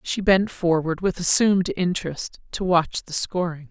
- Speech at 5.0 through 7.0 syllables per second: No, 4.6 syllables/s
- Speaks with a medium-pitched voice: Yes, medium, 180 Hz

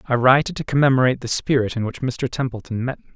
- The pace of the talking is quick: Yes, fast, 245 wpm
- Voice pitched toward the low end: Yes, low, 130 Hz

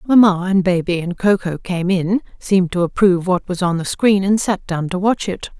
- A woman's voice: Yes, female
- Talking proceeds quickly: Yes, fast, 235 wpm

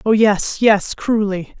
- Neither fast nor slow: Yes, average, 150 wpm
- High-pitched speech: Yes, high, 210 Hz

